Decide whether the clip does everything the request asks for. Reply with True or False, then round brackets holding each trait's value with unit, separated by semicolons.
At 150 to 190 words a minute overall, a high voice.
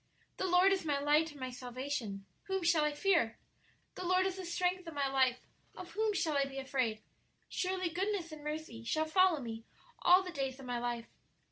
False (205 wpm; 305 Hz)